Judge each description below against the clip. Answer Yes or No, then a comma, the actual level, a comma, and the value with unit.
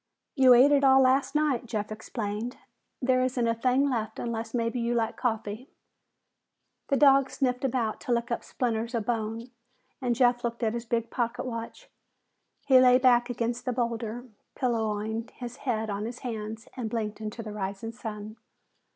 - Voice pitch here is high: Yes, high, 235 Hz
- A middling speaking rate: Yes, average, 170 wpm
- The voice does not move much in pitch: Yes, narrow, 2.2 semitones